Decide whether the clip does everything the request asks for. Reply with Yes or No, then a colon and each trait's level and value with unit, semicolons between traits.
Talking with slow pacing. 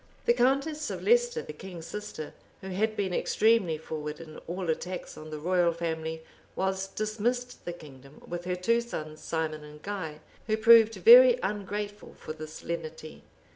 No: average, 165 wpm